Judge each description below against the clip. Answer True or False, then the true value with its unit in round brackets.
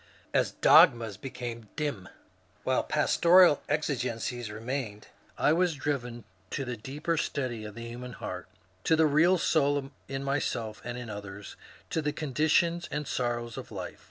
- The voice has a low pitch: True (130 Hz)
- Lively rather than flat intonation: False (4.2 semitones)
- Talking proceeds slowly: False (155 wpm)